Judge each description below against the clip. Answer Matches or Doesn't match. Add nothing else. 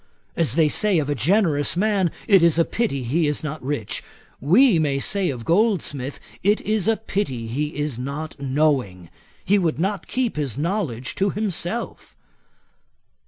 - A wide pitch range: Matches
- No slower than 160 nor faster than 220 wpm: Matches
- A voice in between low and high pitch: Matches